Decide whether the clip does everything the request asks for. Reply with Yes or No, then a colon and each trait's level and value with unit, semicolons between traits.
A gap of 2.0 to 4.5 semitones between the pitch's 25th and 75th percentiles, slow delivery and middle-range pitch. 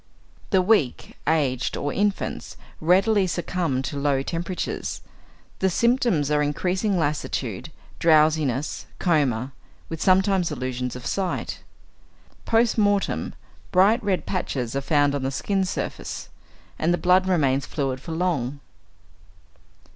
No: average, 5.3 semitones; slow, 125 wpm; medium, 160 Hz